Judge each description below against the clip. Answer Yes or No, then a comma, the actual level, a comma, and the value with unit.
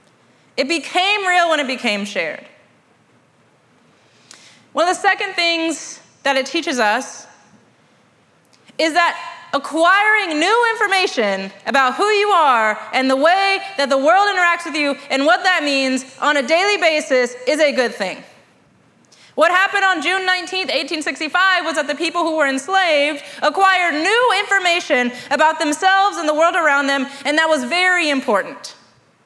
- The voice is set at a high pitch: Yes, very high, 325 Hz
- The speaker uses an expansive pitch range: No, average, 4.8 semitones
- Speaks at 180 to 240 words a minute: No, average, 150 wpm